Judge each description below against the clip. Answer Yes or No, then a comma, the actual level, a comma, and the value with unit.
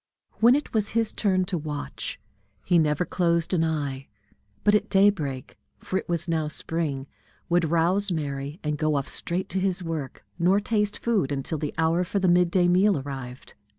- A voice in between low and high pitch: Yes, medium, 170 Hz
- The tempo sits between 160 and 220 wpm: Yes, average, 185 wpm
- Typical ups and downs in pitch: Yes, average, 4.1 semitones